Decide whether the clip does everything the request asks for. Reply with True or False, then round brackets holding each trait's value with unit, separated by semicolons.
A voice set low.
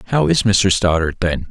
True (85 Hz)